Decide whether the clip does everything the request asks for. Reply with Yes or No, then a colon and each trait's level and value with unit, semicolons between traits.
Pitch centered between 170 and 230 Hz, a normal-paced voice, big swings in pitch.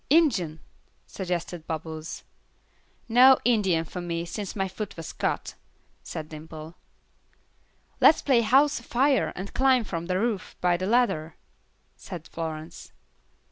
No: medium, 185 Hz; slow, 125 wpm; wide, 6.5 semitones